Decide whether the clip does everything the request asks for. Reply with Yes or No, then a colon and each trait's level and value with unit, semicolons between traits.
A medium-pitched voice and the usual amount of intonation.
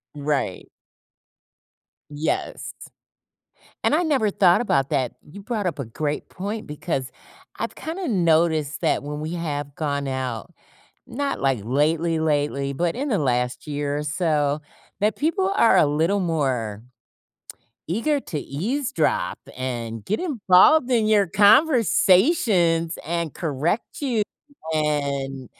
No: medium, 160 Hz; wide, 6.7 semitones